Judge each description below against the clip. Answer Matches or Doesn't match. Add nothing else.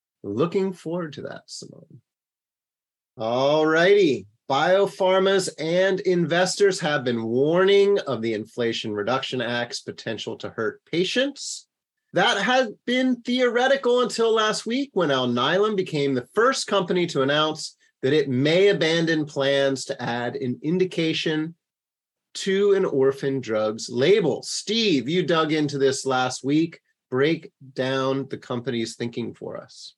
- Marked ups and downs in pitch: Matches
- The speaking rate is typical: Doesn't match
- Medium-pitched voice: Matches